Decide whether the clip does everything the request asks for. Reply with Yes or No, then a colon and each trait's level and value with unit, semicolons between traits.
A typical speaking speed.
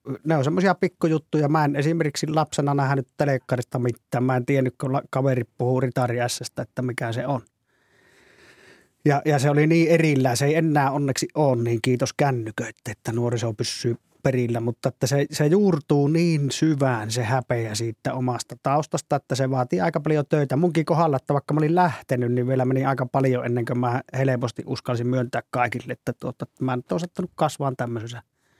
No: fast, 180 wpm